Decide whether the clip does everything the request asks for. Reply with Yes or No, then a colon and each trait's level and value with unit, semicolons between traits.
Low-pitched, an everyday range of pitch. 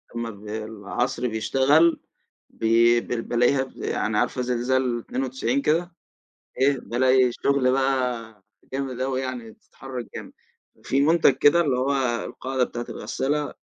No: low, 130 Hz; narrow, 2.3 semitones